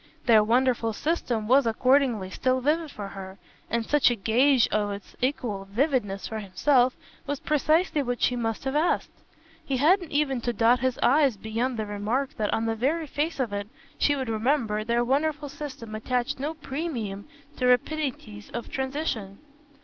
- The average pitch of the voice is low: No, very high, 250 Hz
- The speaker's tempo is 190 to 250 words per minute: No, average, 170 wpm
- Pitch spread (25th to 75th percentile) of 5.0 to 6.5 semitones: No, average, 4.5 semitones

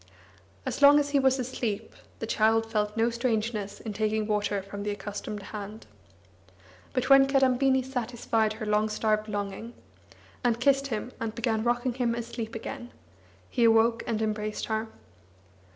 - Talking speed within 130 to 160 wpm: Yes, average, 150 wpm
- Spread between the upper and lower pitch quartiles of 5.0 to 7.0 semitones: No, narrow, 2.6 semitones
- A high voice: Yes, high, 225 Hz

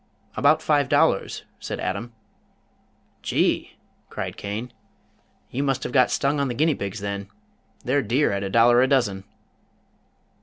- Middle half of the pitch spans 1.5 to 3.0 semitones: No, wide, 5.4 semitones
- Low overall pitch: Yes, low, 125 Hz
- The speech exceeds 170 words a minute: No, average, 145 wpm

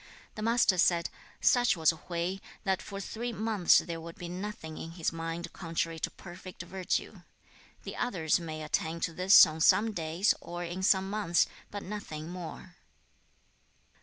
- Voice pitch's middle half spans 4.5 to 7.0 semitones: No, average, 3.1 semitones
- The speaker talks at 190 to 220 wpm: No, average, 160 wpm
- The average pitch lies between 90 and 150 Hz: No, medium, 175 Hz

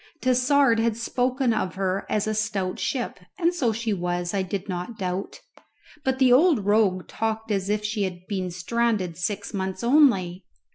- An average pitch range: Yes, average, 4.0 semitones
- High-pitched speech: Yes, high, 210 Hz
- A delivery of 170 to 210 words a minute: Yes, average, 175 wpm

